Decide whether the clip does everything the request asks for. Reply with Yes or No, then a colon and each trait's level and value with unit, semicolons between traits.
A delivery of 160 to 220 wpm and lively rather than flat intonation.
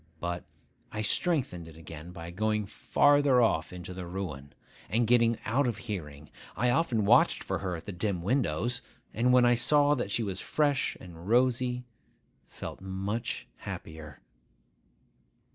No: average, 150 wpm; wide, 5.9 semitones